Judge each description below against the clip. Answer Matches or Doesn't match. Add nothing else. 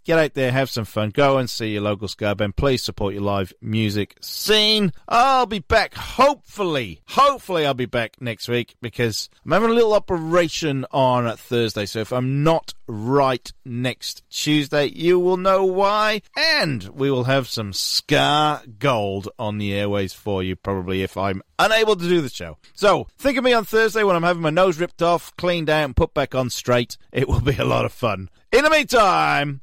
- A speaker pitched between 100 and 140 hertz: Matches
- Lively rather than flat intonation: Matches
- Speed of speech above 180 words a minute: Matches